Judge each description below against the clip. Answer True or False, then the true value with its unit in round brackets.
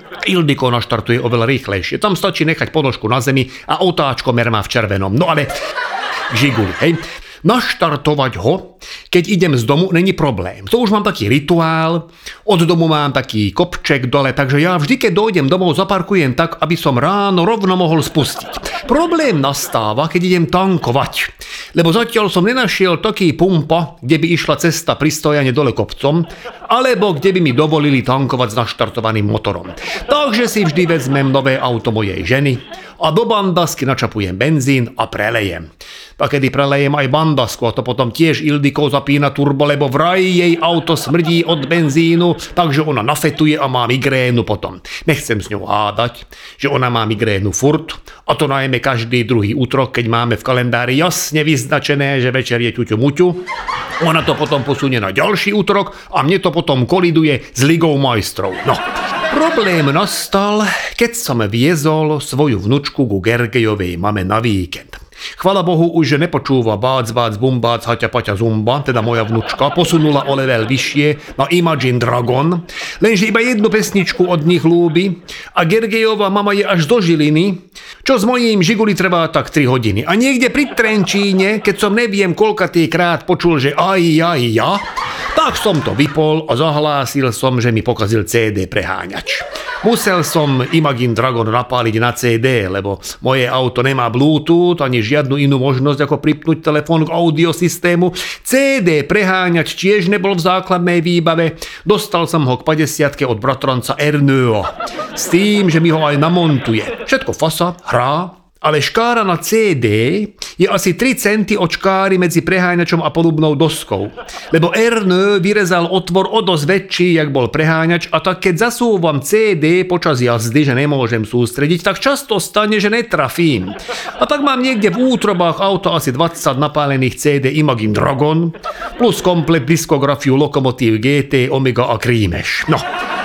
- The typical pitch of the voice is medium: True (155 Hz)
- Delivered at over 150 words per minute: True (160 wpm)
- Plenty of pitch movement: True (5.9 semitones)